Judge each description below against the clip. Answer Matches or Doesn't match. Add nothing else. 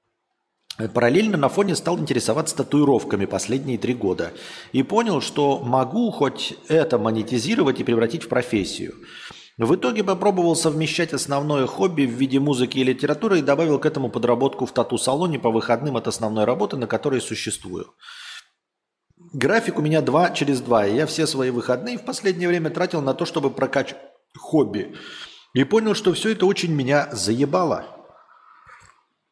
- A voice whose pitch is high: Doesn't match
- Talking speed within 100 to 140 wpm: Doesn't match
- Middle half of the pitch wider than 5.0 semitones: Matches